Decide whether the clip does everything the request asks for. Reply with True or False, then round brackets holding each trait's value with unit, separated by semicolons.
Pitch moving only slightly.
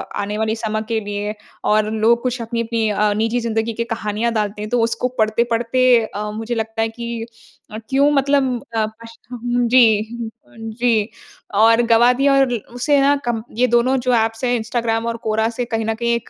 True (1.7 semitones)